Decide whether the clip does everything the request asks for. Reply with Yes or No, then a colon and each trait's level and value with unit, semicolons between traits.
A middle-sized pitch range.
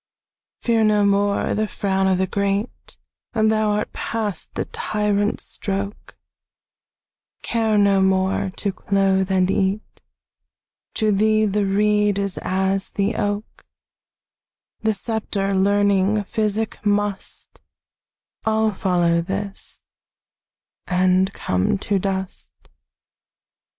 No: narrow, 1.6 semitones